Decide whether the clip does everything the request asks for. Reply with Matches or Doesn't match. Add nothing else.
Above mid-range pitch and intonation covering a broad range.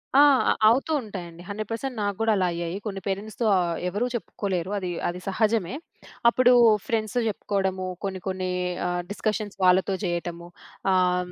Doesn't match